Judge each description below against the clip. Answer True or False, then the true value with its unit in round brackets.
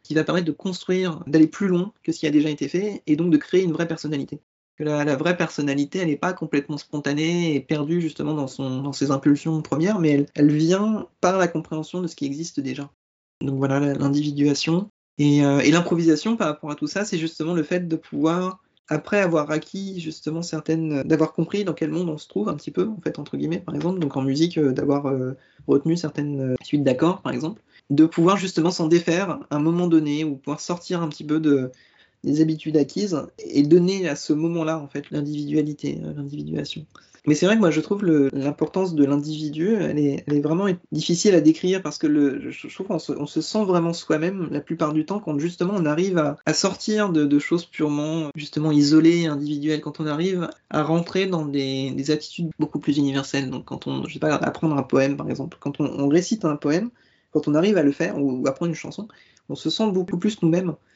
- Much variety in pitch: False (2.9 semitones)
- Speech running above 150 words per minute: True (220 wpm)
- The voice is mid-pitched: True (155 Hz)